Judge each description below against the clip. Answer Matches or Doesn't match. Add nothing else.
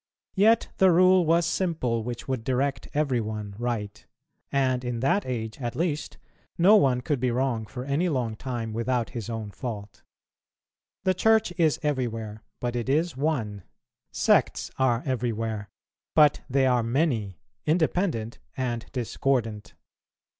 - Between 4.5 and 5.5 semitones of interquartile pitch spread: Matches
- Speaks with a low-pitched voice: Matches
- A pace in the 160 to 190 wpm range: Doesn't match